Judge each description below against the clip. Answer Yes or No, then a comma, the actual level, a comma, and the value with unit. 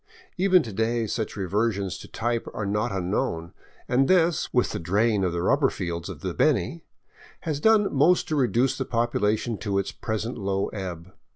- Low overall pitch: Yes, low, 110 Hz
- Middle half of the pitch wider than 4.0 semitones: Yes, average, 4.9 semitones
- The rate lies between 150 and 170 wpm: No, average, 180 wpm